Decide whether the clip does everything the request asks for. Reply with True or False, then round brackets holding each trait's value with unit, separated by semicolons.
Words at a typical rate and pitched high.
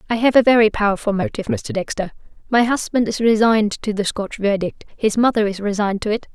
False (210 wpm; 210 Hz)